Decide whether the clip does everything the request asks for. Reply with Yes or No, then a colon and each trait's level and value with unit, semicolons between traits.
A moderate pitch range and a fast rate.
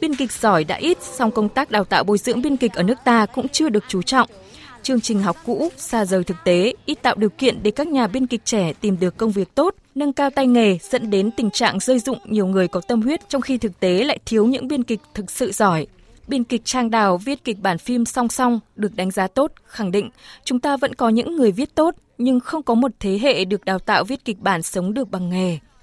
Yes: average, 4.6 semitones; fast, 260 wpm